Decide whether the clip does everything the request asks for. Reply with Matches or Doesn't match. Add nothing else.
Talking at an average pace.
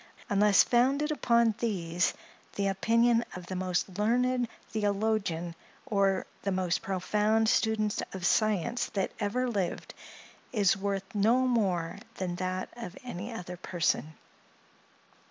Doesn't match